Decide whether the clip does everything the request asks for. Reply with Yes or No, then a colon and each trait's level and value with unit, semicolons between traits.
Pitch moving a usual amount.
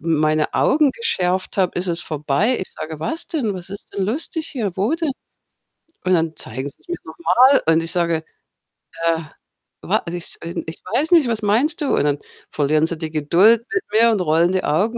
No: wide, 6.5 semitones